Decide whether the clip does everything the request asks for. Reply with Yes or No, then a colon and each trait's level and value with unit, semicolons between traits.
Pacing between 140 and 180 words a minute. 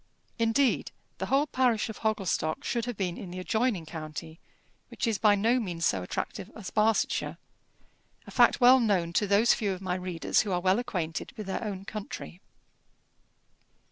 Yes: average, 175 wpm